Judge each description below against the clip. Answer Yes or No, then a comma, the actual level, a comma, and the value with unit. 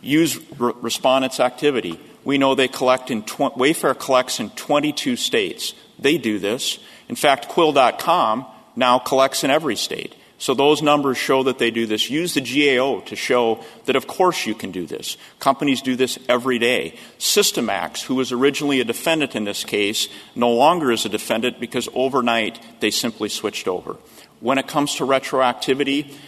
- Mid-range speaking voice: No, low, 130 Hz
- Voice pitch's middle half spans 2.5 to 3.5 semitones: Yes, average, 3.2 semitones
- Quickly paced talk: No, average, 170 wpm